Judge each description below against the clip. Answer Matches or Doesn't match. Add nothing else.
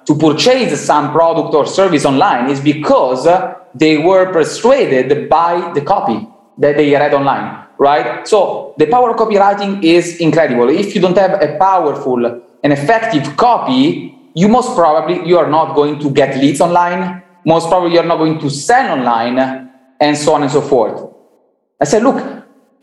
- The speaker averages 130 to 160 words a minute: Doesn't match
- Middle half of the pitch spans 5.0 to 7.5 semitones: Matches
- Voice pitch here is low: Doesn't match